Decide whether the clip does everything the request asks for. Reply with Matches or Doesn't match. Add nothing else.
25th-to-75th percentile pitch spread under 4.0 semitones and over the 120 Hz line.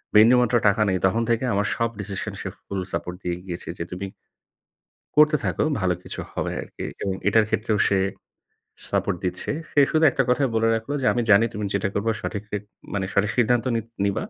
Doesn't match